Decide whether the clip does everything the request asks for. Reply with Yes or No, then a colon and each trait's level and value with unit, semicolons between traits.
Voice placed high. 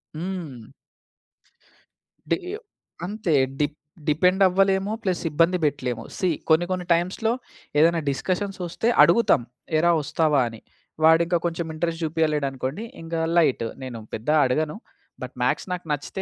No: medium, 165 Hz